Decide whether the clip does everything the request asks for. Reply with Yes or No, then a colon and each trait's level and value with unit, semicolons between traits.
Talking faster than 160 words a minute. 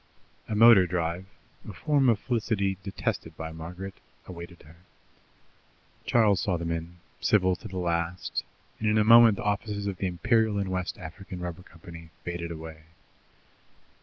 No: average, 155 wpm